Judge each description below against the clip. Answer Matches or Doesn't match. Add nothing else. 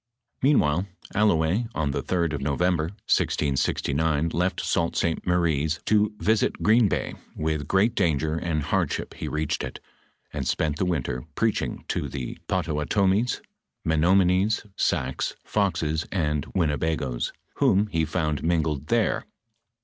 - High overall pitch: Doesn't match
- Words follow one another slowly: Matches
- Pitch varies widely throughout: Doesn't match